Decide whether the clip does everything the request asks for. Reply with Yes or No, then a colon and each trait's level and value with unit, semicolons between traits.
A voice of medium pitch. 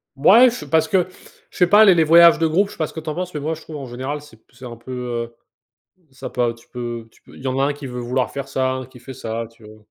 No: low, 130 Hz